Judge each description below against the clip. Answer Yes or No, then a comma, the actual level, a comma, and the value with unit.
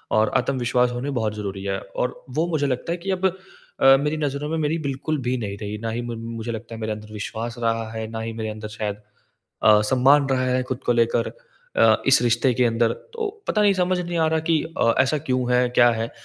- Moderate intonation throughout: Yes, average, 4.2 semitones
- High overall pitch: No, low, 120 Hz